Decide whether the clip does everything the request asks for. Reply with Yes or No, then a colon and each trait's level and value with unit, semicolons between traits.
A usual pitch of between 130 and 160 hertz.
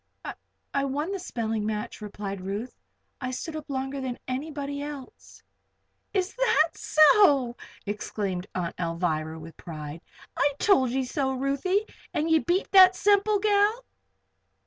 No: very high, 270 Hz